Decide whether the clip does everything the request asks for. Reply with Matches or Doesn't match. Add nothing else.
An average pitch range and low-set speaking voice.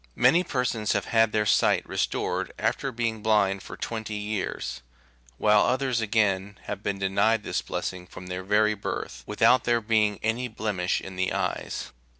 Doesn't match